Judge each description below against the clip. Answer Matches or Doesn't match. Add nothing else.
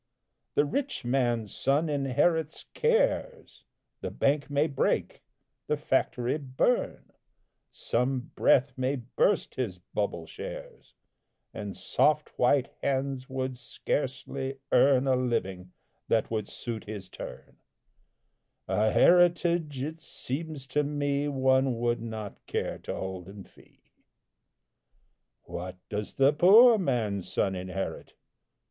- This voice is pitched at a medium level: Doesn't match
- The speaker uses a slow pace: Matches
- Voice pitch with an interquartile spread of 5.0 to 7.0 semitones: Doesn't match